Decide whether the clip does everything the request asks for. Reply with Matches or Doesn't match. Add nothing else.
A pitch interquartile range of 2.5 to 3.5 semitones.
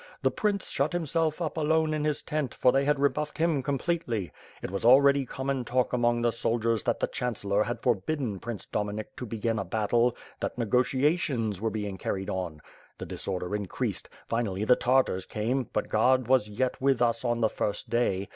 Doesn't match